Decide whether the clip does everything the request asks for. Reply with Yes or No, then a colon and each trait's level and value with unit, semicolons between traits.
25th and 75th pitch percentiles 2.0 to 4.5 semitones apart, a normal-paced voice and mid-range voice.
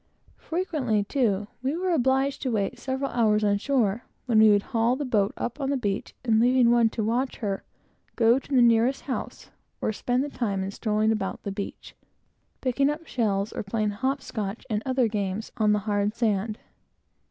No: average, 3.8 semitones; average, 190 wpm; high, 230 Hz